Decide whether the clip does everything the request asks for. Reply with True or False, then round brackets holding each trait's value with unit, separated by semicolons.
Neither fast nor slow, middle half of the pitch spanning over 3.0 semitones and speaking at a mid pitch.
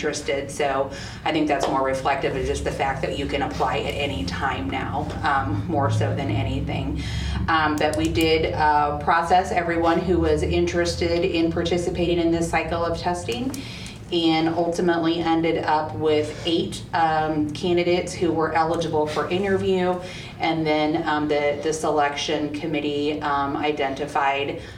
False (150 wpm; 2.4 semitones; 155 Hz)